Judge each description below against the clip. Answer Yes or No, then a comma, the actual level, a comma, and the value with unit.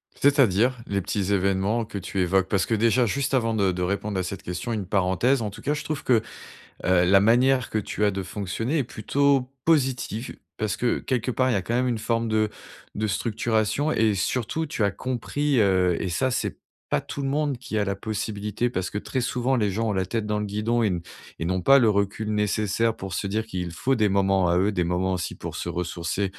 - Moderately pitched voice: No, low, 105 Hz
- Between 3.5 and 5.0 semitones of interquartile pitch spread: Yes, average, 4.1 semitones